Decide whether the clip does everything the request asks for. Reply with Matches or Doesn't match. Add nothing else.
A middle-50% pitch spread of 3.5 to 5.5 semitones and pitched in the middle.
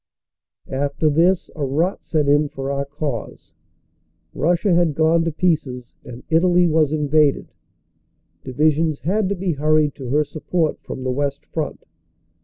Doesn't match